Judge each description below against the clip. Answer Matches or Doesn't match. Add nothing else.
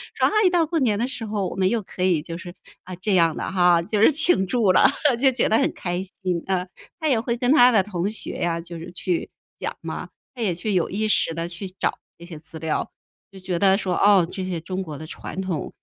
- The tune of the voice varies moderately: Matches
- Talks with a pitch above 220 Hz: Doesn't match